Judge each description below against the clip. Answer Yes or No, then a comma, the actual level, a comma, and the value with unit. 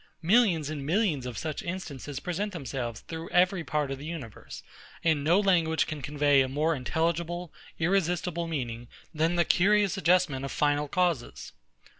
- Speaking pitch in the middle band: Yes, medium, 160 Hz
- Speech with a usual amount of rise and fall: Yes, average, 3.8 semitones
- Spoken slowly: No, average, 155 wpm